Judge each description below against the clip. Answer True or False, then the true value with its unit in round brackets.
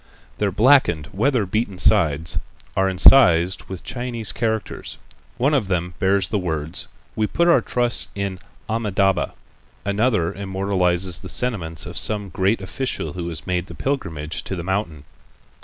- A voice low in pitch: True (95 Hz)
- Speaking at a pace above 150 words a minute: False (145 wpm)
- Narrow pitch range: False (4.1 semitones)